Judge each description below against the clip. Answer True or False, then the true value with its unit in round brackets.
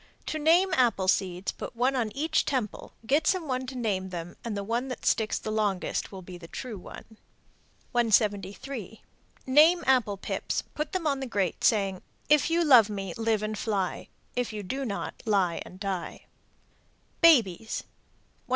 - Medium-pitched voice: False (225 Hz)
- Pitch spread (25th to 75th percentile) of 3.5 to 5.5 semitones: True (5.2 semitones)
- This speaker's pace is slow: False (170 wpm)